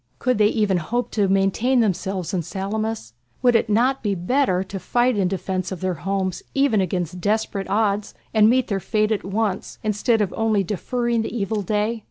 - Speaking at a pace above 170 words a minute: Yes, average, 190 wpm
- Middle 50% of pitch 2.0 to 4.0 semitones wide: Yes, average, 2.8 semitones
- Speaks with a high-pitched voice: Yes, high, 210 Hz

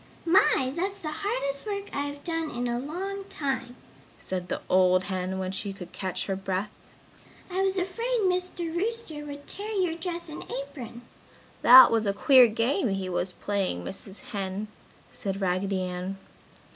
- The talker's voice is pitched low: No, very high, 260 Hz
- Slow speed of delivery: No, average, 165 wpm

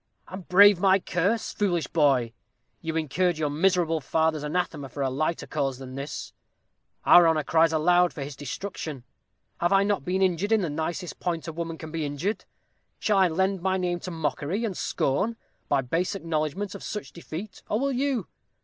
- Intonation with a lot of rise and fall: No, average, 3.8 semitones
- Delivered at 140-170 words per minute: No, average, 185 wpm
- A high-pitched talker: No, medium, 170 Hz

